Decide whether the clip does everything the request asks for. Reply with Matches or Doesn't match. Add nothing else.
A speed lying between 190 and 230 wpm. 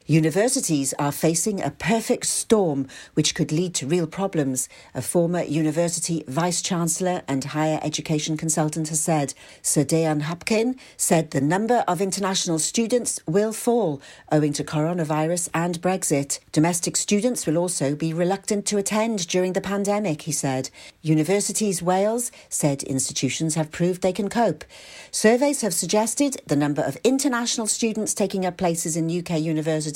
Doesn't match